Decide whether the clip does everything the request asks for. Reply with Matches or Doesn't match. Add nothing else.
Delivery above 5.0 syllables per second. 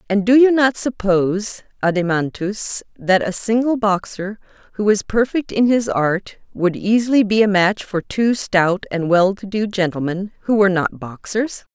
Doesn't match